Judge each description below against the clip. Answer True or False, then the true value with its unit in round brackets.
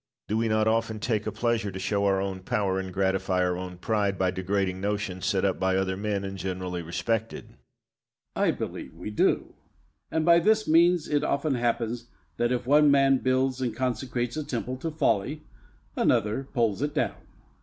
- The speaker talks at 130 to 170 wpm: False (190 wpm)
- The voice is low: True (110 Hz)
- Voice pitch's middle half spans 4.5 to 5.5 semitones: True (5.2 semitones)